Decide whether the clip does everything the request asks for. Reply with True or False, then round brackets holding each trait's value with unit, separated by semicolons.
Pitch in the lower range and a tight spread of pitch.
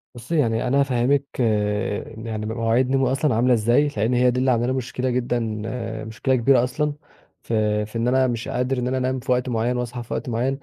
True (125 Hz; 2.0 semitones)